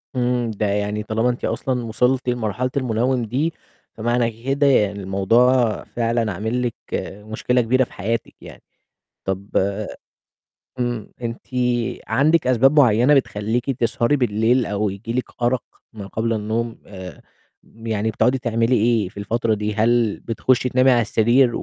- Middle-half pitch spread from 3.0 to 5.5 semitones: No, narrow, 2.5 semitones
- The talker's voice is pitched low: Yes, low, 115 Hz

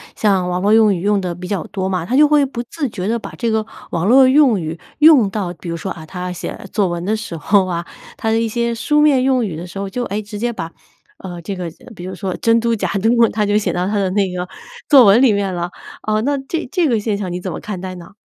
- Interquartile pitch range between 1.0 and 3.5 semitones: No, average, 4.3 semitones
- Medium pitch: No, high, 205 Hz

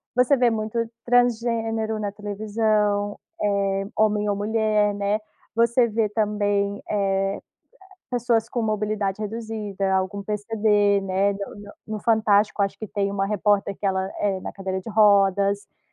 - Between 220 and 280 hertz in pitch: No, high, 210 Hz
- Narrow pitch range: Yes, narrow, 1.7 semitones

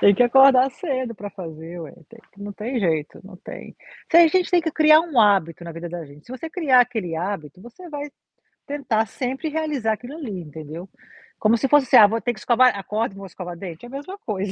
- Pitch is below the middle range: No, high, 225 Hz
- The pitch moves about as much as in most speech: No, wide, 6.8 semitones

